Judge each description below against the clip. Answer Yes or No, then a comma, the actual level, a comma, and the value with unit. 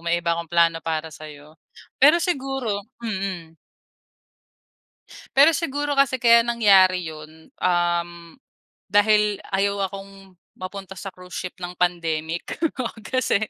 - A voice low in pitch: No, high, 190 Hz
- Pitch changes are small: No, average, 4.2 semitones